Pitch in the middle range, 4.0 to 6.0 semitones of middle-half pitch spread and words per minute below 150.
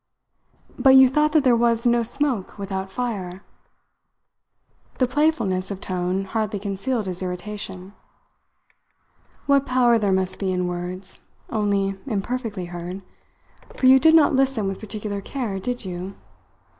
No: high, 205 Hz; average, 4.8 semitones; slow, 135 wpm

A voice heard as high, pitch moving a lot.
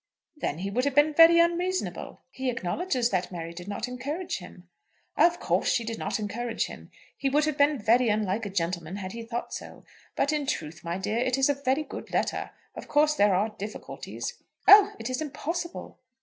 Yes: very high, 250 Hz; wide, 6.7 semitones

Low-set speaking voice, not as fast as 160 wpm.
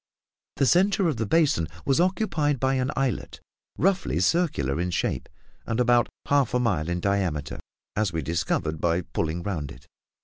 No: low, 115 Hz; average, 165 wpm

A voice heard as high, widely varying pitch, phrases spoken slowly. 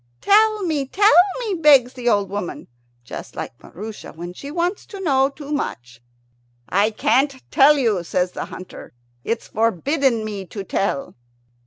No: very high, 250 Hz; wide, 7.1 semitones; average, 155 wpm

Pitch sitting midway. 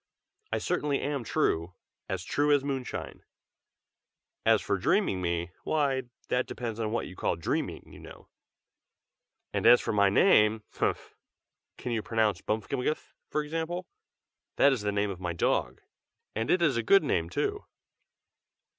No: low, 115 Hz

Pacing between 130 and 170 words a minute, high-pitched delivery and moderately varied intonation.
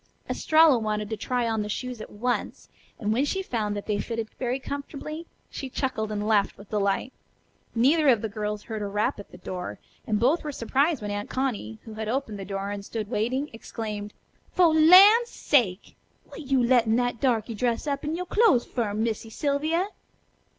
No: average, 190 wpm; high, 230 Hz; average, 4.9 semitones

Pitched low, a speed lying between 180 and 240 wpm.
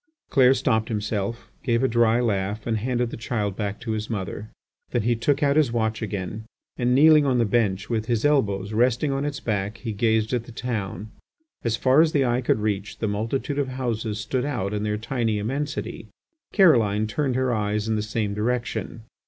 Yes: low, 115 Hz; average, 200 wpm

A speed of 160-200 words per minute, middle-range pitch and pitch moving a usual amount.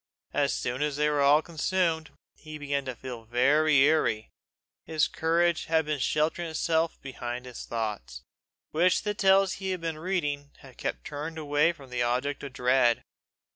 Yes: average, 170 wpm; medium, 150 Hz; average, 4.2 semitones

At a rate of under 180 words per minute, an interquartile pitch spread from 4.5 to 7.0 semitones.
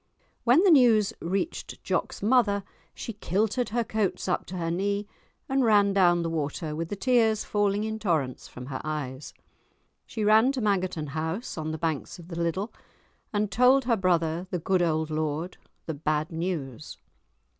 Yes: average, 170 wpm; average, 5.2 semitones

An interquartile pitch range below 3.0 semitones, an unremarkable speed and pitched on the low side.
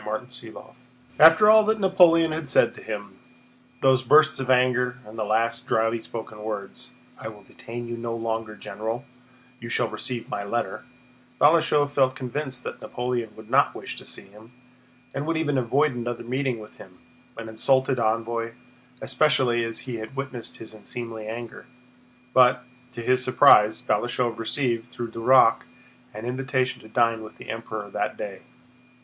Yes: narrow, 2.5 semitones; average, 155 wpm; low, 120 Hz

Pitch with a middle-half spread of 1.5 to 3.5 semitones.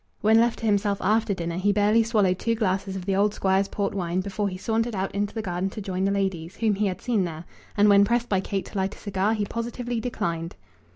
Yes: narrow, 2.5 semitones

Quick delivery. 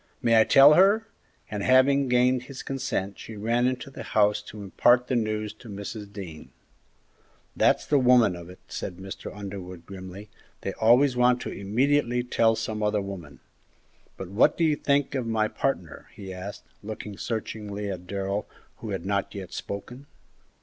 No: average, 170 wpm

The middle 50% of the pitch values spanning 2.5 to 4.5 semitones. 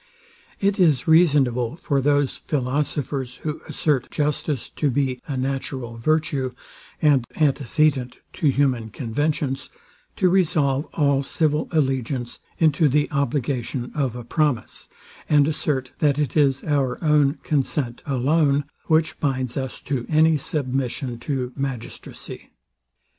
Yes: average, 2.8 semitones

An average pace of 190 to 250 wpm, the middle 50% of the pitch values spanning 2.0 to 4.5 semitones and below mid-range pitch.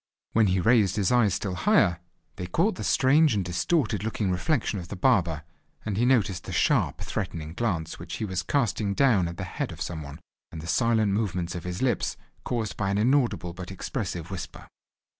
No: average, 195 wpm; average, 4.9 semitones; low, 100 Hz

